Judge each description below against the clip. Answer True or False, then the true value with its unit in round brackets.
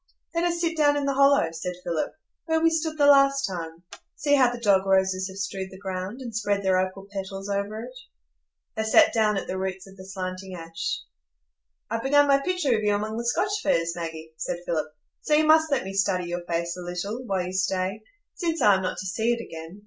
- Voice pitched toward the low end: False (200 Hz)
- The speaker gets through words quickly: True (225 wpm)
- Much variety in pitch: True (6.9 semitones)